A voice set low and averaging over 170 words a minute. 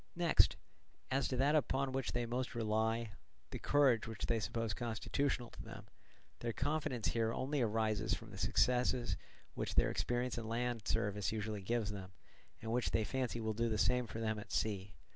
Yes: low, 115 Hz; average, 180 wpm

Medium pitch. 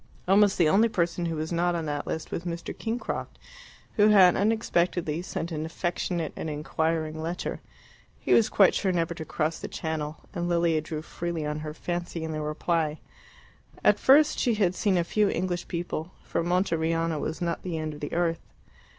Yes: medium, 170 Hz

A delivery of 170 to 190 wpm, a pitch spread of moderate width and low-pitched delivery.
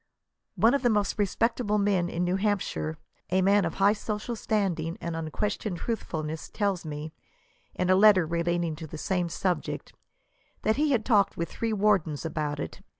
No: average, 175 wpm; average, 4.2 semitones; high, 190 Hz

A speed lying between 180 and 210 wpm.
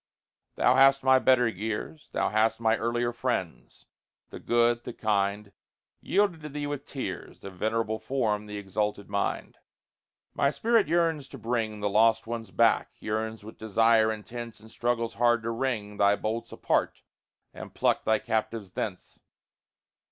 No: average, 150 wpm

